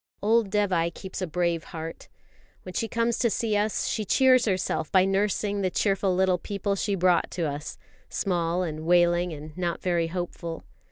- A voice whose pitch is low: No, medium, 185 Hz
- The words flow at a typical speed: Yes, average, 175 wpm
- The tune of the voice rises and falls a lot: No, average, 3.0 semitones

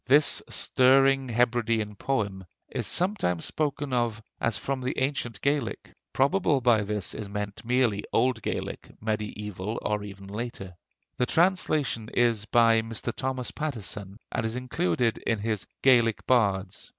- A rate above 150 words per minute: No, average, 140 wpm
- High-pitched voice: No, low, 115 Hz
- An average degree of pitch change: Yes, average, 3.8 semitones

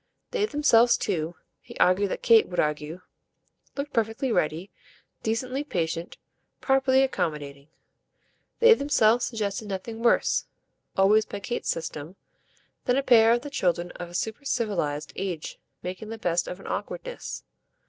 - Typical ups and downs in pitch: No, wide, 5.9 semitones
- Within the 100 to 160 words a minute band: Yes, average, 140 wpm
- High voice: Yes, high, 215 Hz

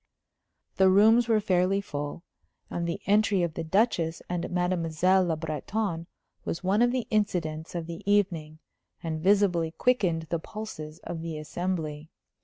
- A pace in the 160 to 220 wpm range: No, average, 150 wpm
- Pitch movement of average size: Yes, average, 3.8 semitones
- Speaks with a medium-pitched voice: Yes, medium, 175 Hz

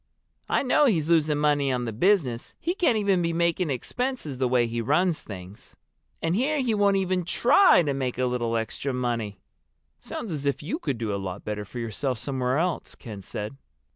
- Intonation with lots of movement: Yes, wide, 7.5 semitones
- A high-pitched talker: No, medium, 140 Hz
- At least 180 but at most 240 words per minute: Yes, average, 200 wpm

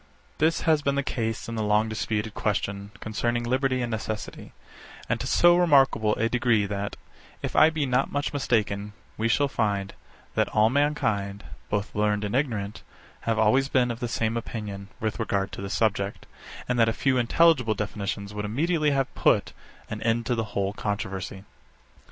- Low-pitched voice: Yes, low, 110 Hz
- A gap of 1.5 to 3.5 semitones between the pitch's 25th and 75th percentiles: No, average, 3.9 semitones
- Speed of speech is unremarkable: Yes, average, 180 wpm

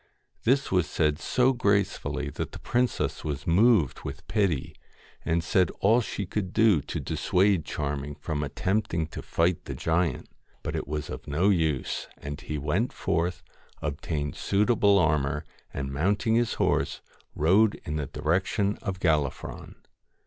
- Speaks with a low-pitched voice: Yes, very low, 85 Hz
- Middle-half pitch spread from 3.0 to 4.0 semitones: No, wide, 5.5 semitones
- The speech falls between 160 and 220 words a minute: No, average, 140 wpm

